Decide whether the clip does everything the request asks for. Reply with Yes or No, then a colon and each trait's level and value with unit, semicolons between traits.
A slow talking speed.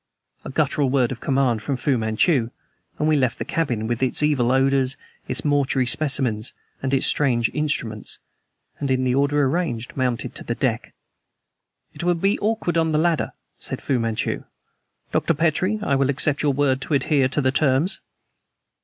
No: average, 175 wpm